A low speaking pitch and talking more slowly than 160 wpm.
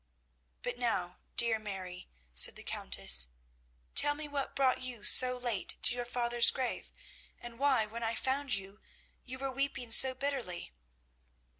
No: high, 240 Hz; average, 150 wpm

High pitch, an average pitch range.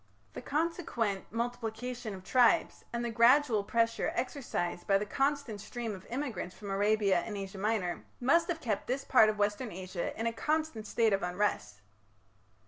Yes: high, 225 Hz; average, 3.9 semitones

